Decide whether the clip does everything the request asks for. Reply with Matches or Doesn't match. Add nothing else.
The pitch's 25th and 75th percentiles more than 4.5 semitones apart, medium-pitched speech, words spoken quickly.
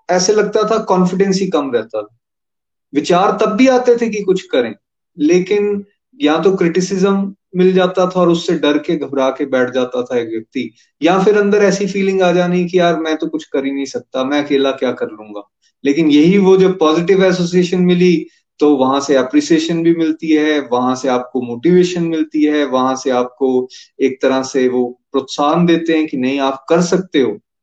Matches